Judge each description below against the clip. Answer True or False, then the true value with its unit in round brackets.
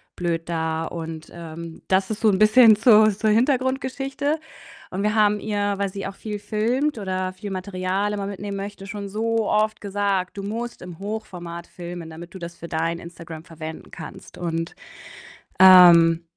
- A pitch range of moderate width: True (3.8 semitones)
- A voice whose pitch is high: True (195 Hz)